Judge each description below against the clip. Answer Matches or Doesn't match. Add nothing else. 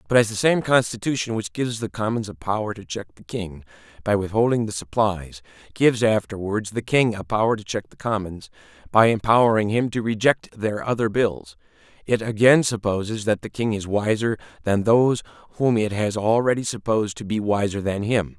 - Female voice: Doesn't match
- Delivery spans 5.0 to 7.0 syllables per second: Matches